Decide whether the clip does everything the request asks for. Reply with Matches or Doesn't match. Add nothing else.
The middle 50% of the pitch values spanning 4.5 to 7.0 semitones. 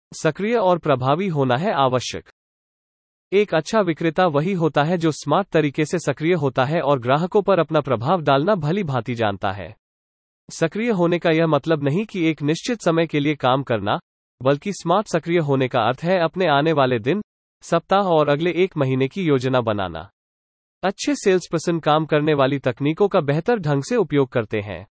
Matches